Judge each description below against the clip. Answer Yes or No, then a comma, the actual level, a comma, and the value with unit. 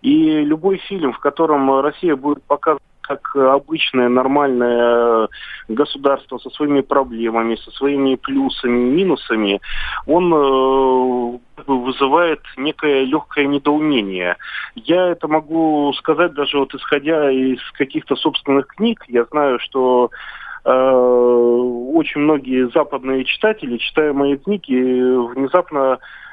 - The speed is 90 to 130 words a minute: Yes, slow, 110 wpm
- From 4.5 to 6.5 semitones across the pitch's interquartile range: No, average, 3.1 semitones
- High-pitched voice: No, medium, 140 Hz